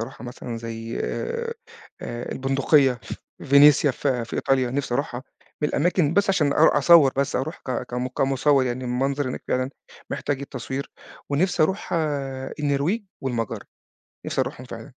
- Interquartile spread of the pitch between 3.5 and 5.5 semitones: No, average, 2.9 semitones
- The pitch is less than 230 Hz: Yes, low, 135 Hz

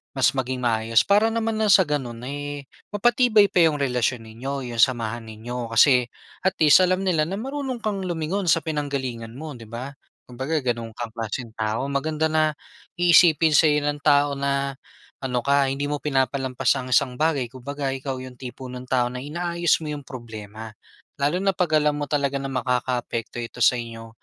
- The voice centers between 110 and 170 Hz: Yes, medium, 140 Hz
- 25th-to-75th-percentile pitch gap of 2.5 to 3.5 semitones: No, average, 4.2 semitones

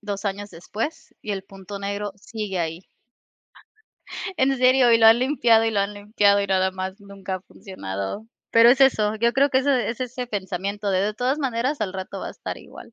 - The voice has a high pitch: Yes, high, 210 Hz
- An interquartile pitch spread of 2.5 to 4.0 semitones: Yes, average, 3.6 semitones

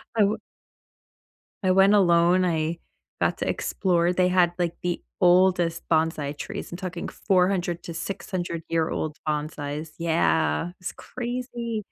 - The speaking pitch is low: No, medium, 175 Hz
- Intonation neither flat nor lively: No, narrow, 2.2 semitones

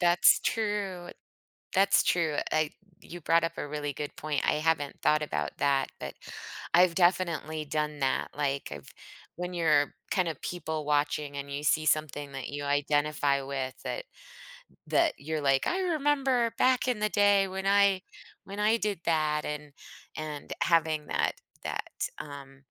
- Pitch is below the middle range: No, medium, 155 Hz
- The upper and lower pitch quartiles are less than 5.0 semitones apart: Yes, average, 4.6 semitones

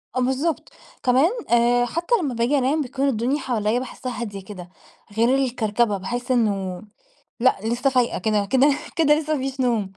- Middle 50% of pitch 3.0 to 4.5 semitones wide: Yes, average, 3.5 semitones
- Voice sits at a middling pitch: No, high, 245 Hz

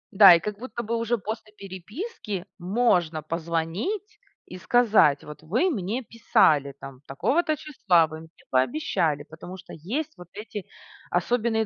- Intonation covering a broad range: Yes, wide, 6.4 semitones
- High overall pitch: Yes, high, 195 Hz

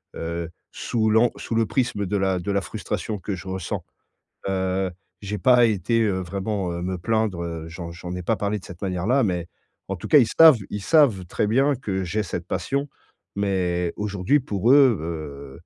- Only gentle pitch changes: No, average, 3.9 semitones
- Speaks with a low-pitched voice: Yes, low, 100 Hz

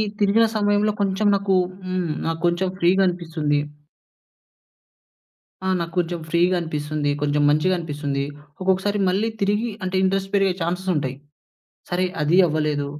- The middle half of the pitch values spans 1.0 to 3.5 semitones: No, average, 4.0 semitones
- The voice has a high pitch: No, medium, 180 Hz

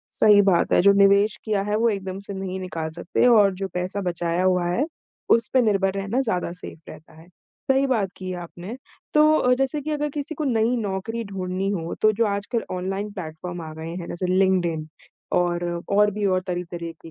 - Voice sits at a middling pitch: No, high, 195 Hz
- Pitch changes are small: No, average, 3.4 semitones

